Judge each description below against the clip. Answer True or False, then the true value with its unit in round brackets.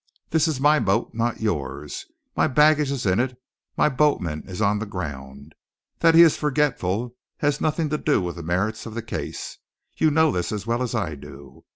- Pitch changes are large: True (8.8 semitones)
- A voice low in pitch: True (115 Hz)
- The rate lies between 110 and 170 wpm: False (200 wpm)